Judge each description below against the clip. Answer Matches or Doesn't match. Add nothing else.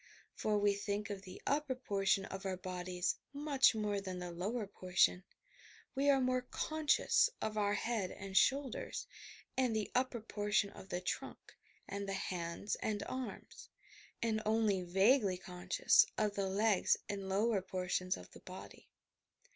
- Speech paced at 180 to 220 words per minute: Doesn't match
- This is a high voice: Matches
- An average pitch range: Matches